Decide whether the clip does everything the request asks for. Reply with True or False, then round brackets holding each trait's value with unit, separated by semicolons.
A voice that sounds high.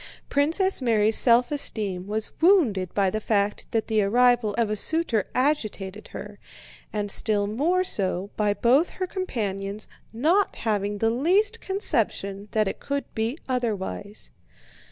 True (220 Hz)